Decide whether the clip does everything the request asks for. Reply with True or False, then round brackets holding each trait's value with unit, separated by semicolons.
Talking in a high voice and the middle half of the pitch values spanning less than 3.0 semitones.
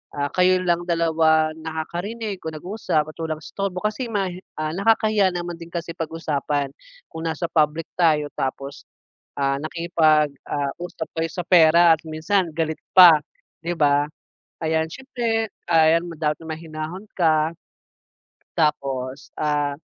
False (160 Hz; 2.5 semitones)